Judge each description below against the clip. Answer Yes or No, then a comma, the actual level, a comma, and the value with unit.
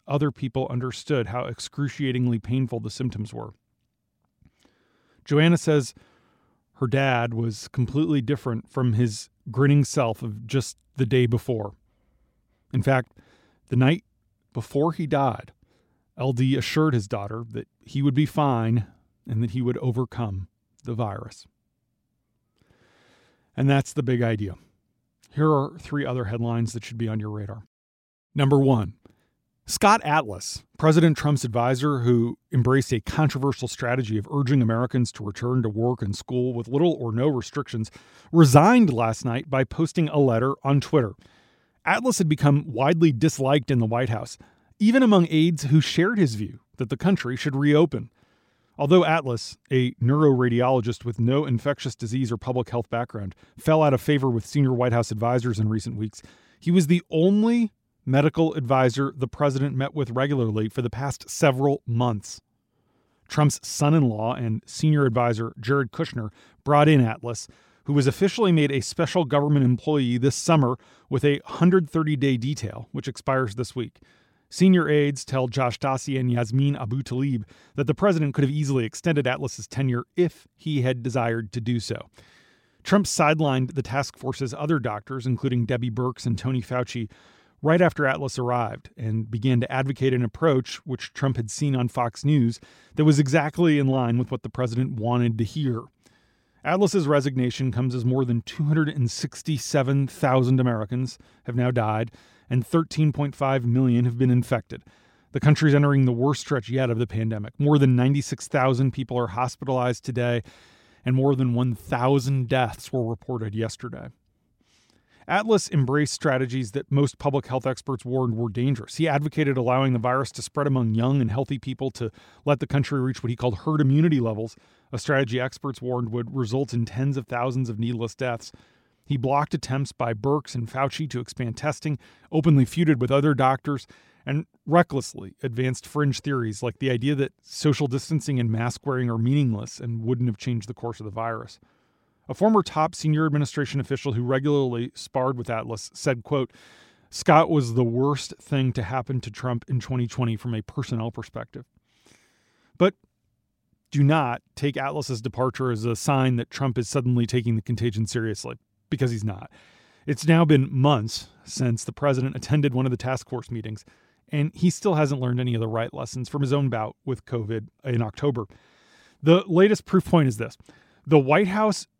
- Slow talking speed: No, average, 165 wpm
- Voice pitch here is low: Yes, low, 130 Hz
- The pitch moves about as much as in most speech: Yes, average, 3.2 semitones